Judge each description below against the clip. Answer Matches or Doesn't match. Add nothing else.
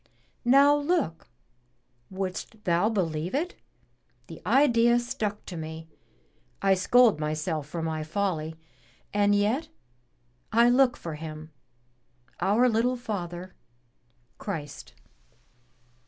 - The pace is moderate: Doesn't match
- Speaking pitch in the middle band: Doesn't match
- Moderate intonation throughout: Doesn't match